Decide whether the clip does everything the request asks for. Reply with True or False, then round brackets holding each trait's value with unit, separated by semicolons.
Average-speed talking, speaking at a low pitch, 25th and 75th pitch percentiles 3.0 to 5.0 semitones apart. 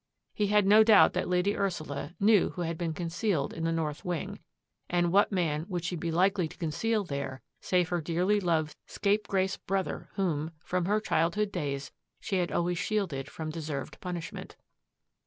False (175 wpm; 175 Hz; 3.6 semitones)